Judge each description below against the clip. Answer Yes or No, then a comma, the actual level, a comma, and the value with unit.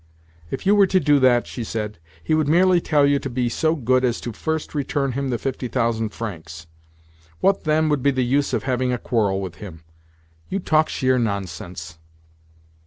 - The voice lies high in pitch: No, low, 130 Hz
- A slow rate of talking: No, average, 195 wpm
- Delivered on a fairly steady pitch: No, average, 5.1 semitones